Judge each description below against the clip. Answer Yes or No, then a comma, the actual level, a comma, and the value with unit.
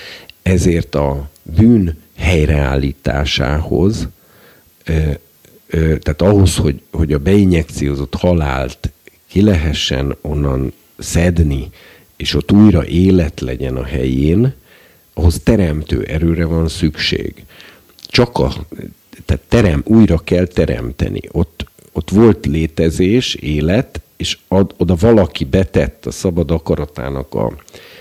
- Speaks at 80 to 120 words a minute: Yes, slow, 105 wpm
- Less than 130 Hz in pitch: Yes, very low, 80 Hz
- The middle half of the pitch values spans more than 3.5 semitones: Yes, average, 4.0 semitones